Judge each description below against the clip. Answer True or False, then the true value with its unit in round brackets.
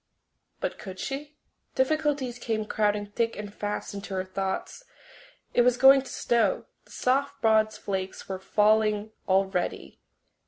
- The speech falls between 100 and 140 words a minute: True (135 wpm)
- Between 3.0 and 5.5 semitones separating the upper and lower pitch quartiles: True (4.2 semitones)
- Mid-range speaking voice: False (215 Hz)